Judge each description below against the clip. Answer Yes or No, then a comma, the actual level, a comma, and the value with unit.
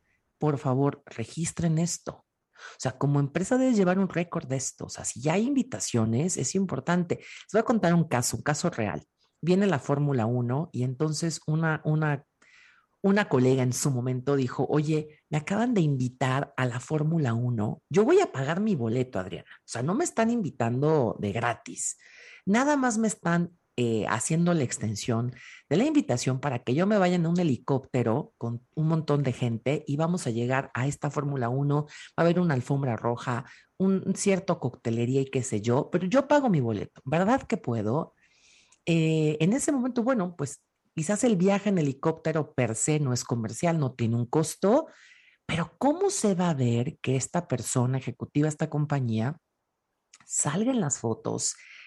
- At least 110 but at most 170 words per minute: No, average, 185 wpm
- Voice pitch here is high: No, medium, 150 Hz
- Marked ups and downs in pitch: Yes, wide, 6.2 semitones